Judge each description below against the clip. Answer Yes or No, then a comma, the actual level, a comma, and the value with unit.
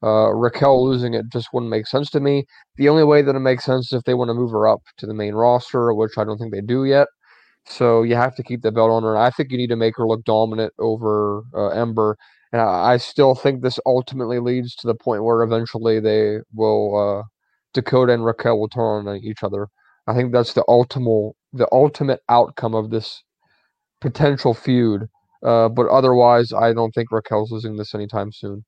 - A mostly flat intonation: Yes, narrow, 2.3 semitones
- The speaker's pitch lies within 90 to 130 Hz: Yes, low, 115 Hz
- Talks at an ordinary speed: No, fast, 220 wpm